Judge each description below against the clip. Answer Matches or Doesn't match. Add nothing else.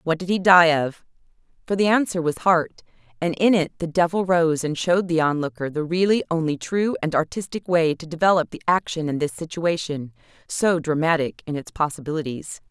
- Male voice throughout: Doesn't match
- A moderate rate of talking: Matches